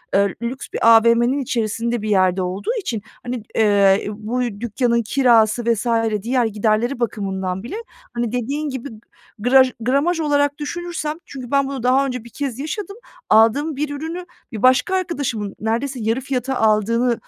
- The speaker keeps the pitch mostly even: No, average, 4.0 semitones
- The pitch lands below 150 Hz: No, high, 240 Hz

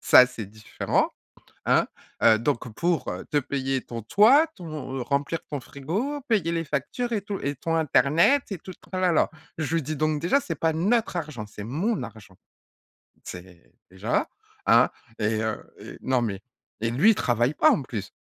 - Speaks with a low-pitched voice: No, medium, 145 Hz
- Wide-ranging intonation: Yes, wide, 6.6 semitones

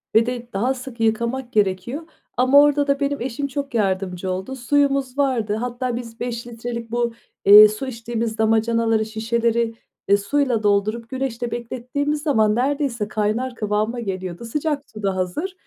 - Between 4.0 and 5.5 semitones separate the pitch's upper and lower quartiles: No, average, 3.4 semitones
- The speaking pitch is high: Yes, high, 235 Hz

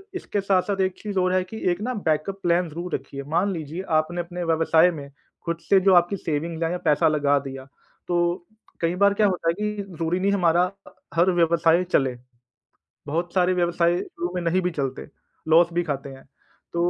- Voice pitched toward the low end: No, medium, 175 Hz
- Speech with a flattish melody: Yes, narrow, 2.2 semitones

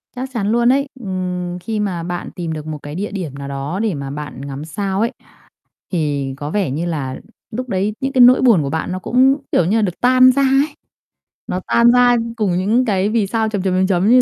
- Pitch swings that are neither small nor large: No, wide, 6.6 semitones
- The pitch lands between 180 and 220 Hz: Yes, high, 190 Hz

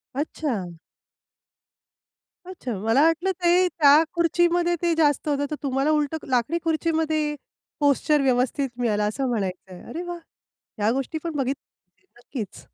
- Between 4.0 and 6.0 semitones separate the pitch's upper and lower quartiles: Yes, average, 4.8 semitones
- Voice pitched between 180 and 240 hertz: No, very high, 290 Hz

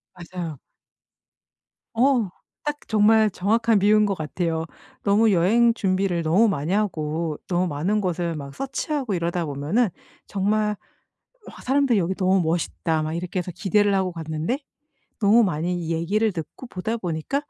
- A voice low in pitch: No, medium, 185 Hz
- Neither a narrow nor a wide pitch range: Yes, average, 4.3 semitones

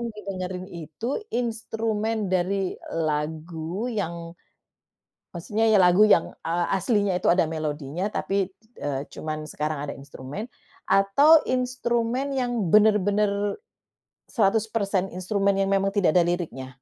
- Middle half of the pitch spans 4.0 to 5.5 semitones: Yes, average, 4.4 semitones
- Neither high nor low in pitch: No, high, 195 Hz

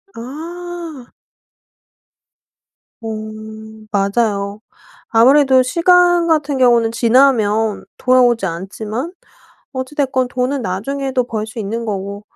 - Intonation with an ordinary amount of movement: Yes, average, 4.3 semitones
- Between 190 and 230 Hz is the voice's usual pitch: No, very high, 250 Hz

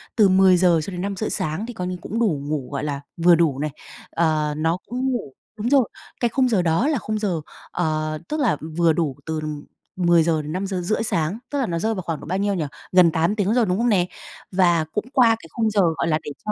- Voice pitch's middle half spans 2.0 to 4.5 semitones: No, average, 5.0 semitones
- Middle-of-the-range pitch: Yes, medium, 180 Hz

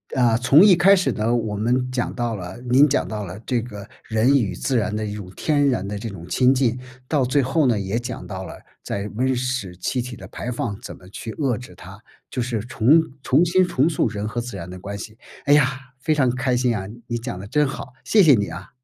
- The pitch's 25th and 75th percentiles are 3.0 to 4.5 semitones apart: Yes, average, 4.1 semitones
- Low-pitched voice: Yes, low, 120 Hz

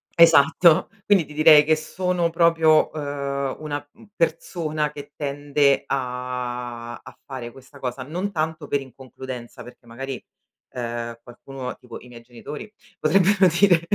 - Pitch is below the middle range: No, medium, 145 Hz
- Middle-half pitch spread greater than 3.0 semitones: Yes, average, 4.2 semitones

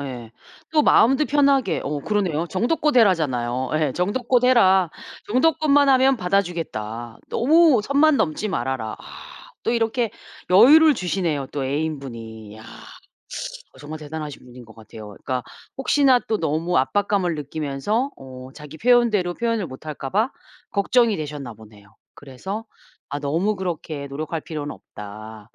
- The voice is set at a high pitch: No, medium, 165 Hz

